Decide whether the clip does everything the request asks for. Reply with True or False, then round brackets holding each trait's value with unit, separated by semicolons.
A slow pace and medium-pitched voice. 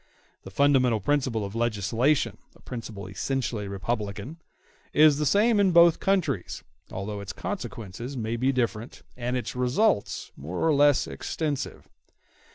False (125 wpm; 125 Hz)